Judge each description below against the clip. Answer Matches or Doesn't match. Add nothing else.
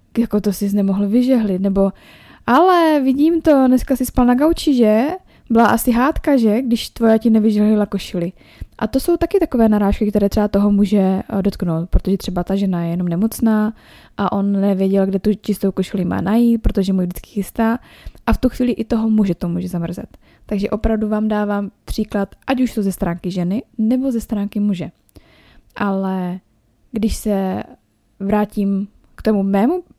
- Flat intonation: Doesn't match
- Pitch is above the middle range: Matches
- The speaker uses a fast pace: Matches